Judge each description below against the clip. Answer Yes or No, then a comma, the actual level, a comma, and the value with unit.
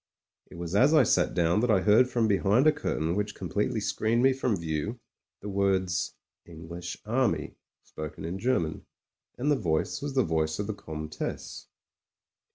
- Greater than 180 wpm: No, average, 165 wpm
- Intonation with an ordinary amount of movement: No, wide, 6.5 semitones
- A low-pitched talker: Yes, low, 100 Hz